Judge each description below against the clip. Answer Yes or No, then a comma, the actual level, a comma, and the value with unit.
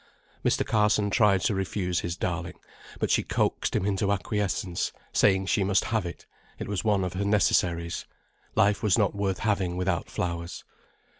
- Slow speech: No, average, 165 wpm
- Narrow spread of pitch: Yes, narrow, 2.3 semitones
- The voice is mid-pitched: No, very low, 95 Hz